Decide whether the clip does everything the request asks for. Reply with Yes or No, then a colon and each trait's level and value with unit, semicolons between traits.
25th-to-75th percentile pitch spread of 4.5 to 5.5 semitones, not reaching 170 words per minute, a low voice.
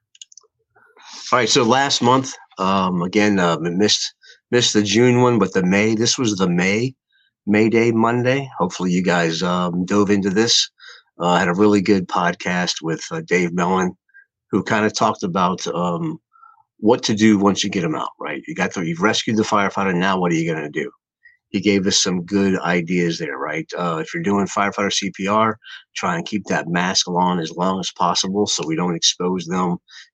No: average, 5.0 semitones; average, 195 wpm; low, 100 Hz